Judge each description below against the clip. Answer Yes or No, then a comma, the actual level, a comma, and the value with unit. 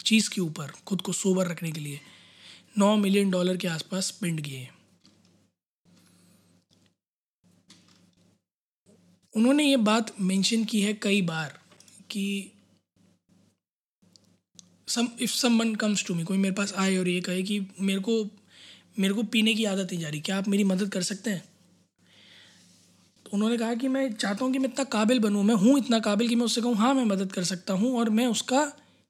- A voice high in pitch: Yes, high, 200 Hz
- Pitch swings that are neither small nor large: Yes, average, 3.7 semitones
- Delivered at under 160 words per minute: No, average, 170 wpm